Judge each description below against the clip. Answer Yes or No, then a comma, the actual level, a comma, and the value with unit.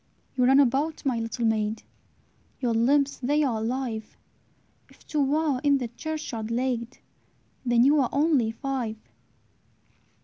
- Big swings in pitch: No, average, 3.5 semitones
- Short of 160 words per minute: Yes, slow, 135 wpm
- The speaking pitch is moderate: No, very high, 255 Hz